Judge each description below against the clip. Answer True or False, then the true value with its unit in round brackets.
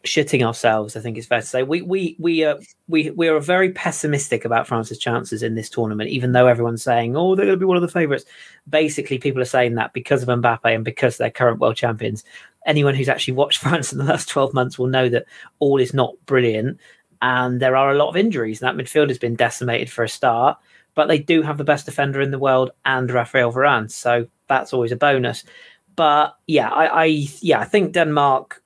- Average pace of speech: False (230 wpm)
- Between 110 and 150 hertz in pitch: True (135 Hz)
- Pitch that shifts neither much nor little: True (4.0 semitones)